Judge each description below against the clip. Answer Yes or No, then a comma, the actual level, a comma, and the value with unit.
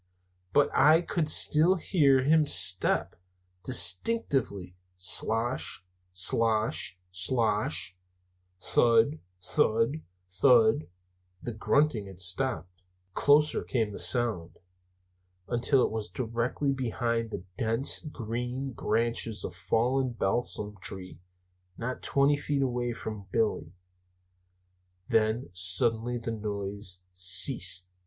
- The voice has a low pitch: Yes, low, 115 Hz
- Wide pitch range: No, average, 4.8 semitones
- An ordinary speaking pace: No, slow, 100 wpm